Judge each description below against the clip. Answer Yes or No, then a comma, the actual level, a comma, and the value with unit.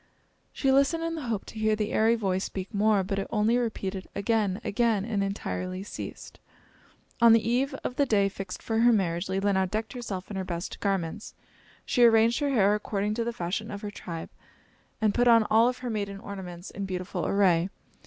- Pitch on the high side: Yes, high, 210 Hz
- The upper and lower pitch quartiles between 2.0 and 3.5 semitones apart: Yes, average, 3.2 semitones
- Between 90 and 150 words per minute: No, average, 200 wpm